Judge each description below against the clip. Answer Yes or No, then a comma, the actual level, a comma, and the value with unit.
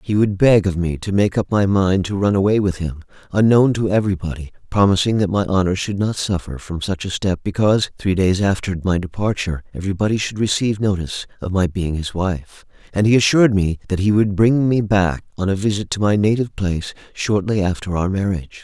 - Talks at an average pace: No, fast, 210 wpm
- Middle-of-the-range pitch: No, very low, 95 Hz